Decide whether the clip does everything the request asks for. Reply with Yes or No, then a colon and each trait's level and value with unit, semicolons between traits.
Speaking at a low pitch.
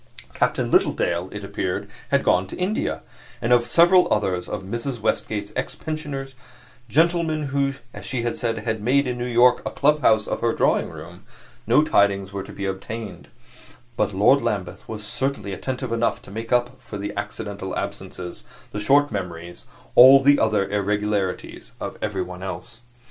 Yes: low, 110 Hz